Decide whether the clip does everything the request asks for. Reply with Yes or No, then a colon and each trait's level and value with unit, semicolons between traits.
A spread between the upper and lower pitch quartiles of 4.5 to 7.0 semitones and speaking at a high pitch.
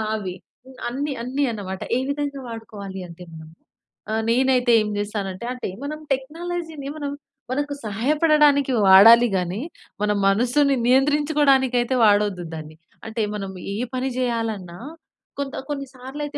Yes: wide, 5.6 semitones; very high, 250 Hz